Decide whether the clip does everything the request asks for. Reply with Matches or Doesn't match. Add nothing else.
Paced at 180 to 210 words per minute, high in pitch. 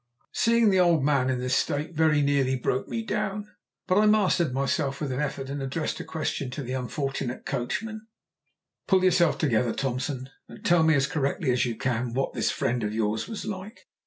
Doesn't match